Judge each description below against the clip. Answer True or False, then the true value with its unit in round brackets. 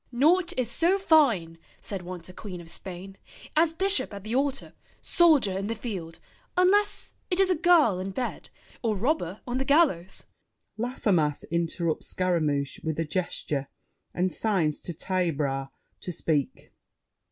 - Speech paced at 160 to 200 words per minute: False (150 wpm)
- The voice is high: True (195 Hz)